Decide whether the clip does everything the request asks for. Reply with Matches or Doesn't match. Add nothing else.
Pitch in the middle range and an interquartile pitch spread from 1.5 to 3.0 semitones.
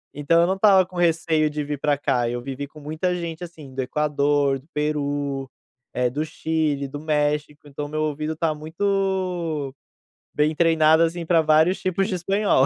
Matches